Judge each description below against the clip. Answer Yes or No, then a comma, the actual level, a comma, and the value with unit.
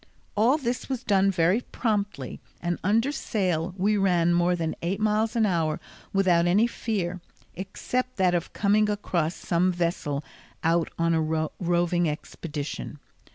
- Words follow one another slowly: No, average, 145 wpm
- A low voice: No, medium, 180 Hz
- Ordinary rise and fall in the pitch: Yes, average, 3.9 semitones